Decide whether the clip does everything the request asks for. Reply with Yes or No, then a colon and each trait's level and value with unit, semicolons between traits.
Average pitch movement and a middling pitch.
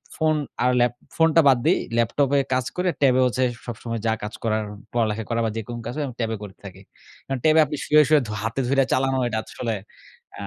No: average, 3.8 semitones; low, 125 Hz